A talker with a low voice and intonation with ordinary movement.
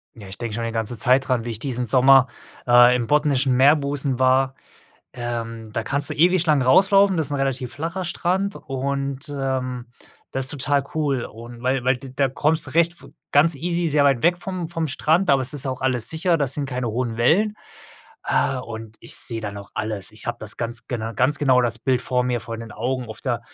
Yes: low, 130 Hz; average, 3.3 semitones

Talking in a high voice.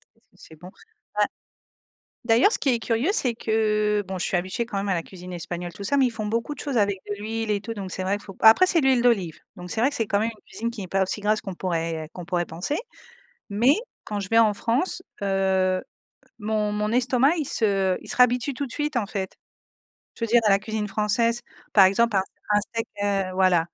Yes: high, 210 Hz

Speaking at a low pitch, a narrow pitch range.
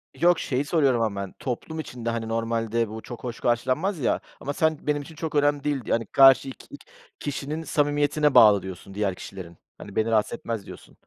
No: low, 125 Hz; average, 4.6 semitones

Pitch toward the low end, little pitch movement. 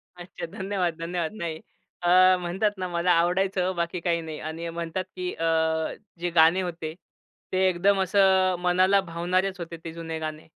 No: medium, 175 Hz; narrow, 2.0 semitones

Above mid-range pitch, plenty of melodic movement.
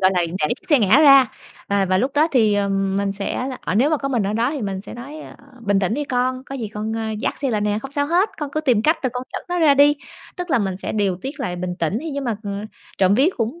Yes: high, 235 Hz; wide, 5.8 semitones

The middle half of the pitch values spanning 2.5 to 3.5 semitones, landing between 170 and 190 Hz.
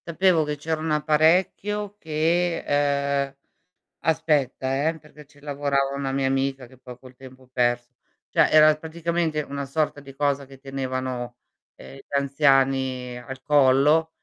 No: average, 2.9 semitones; medium, 140 Hz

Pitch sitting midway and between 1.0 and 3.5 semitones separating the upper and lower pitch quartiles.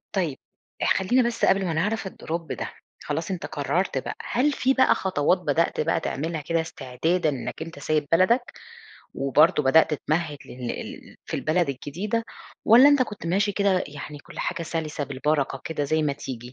No: medium, 165 Hz; average, 4.8 semitones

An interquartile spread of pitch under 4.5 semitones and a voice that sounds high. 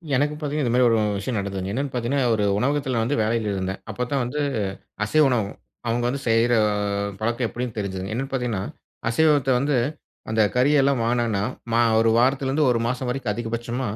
No: average, 3.2 semitones; low, 120 Hz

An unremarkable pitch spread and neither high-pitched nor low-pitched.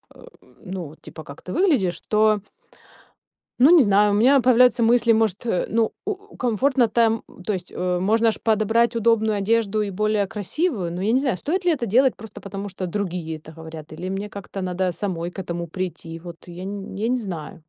No: average, 4.2 semitones; high, 205 Hz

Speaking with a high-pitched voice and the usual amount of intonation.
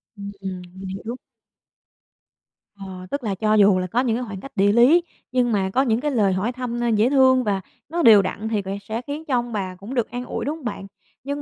Yes: high, 225 Hz; average, 4.4 semitones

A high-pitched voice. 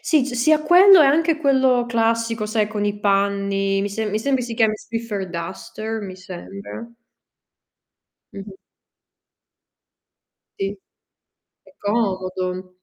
Yes: high, 215 Hz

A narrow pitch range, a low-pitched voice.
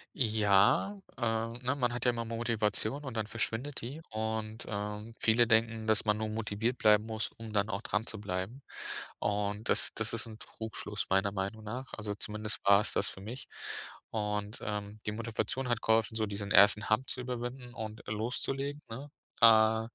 Yes: narrow, 2.0 semitones; low, 110 Hz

